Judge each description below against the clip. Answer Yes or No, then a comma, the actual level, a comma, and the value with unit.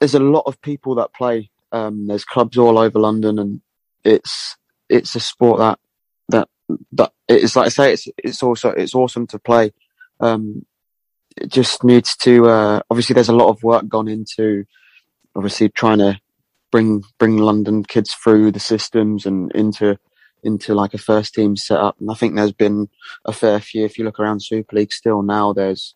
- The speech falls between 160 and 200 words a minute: Yes, average, 190 wpm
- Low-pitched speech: Yes, low, 110 Hz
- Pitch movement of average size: No, narrow, 1.9 semitones